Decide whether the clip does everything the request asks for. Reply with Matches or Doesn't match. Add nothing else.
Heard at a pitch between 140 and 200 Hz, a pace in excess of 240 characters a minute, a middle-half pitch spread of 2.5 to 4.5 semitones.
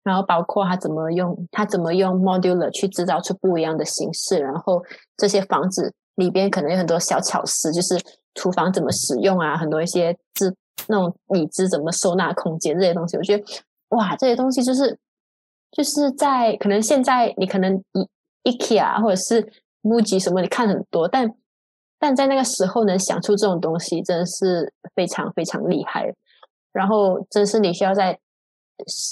Matches